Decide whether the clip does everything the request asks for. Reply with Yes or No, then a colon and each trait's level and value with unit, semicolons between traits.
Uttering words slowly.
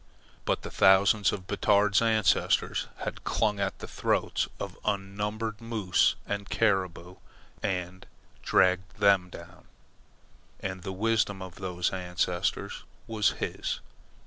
Yes: slow, 120 wpm